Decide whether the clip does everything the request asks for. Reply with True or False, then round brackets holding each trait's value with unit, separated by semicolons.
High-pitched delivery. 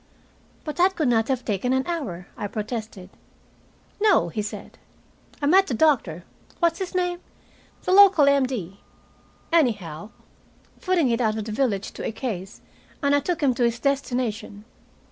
True (250 Hz)